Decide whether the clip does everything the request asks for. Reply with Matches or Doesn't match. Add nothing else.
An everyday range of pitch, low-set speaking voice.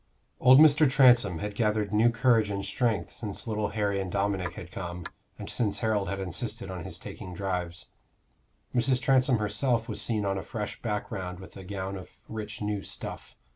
Matches